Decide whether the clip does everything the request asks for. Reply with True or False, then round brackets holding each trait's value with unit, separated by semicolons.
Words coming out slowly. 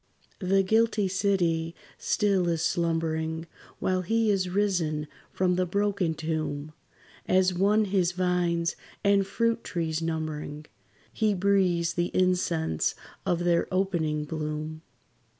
True (115 wpm)